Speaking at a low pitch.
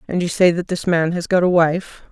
No: medium, 175 Hz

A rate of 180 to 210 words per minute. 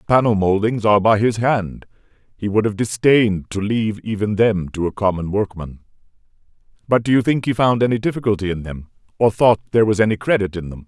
Yes: fast, 205 wpm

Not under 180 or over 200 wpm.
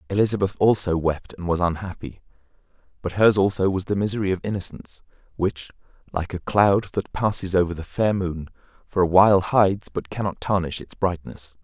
No: average, 170 wpm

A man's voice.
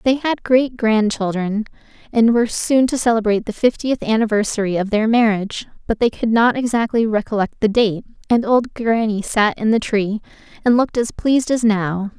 No: female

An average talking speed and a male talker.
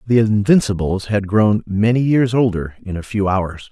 Yes: average, 180 wpm; male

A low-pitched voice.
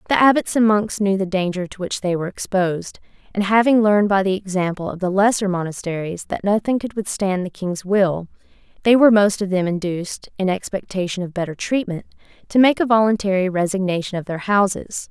No: high, 195 Hz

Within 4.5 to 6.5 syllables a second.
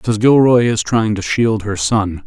No: 4.1 syllables/s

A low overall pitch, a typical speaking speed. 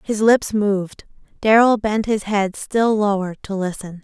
No: high, 205 Hz; average, 165 wpm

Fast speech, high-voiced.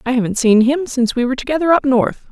Yes: fast, 260 wpm; very high, 260 Hz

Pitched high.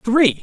Yes: high, 240 Hz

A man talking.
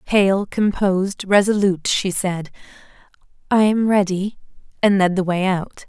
No: female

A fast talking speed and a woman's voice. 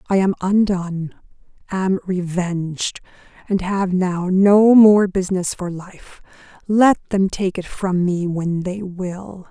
No: average, 140 wpm; female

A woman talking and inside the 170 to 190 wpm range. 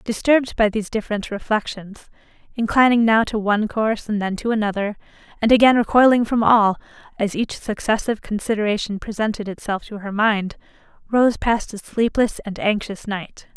No: female; average, 155 wpm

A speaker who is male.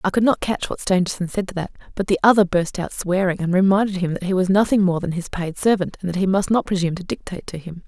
No: female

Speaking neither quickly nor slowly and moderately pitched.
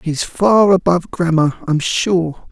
Yes: average, 145 wpm; medium, 175 Hz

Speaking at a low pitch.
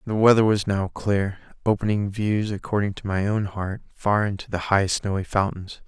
Yes: low, 100 Hz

